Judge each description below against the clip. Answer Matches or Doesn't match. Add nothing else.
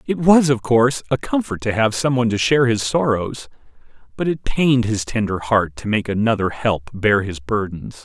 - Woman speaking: Doesn't match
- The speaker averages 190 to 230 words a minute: Matches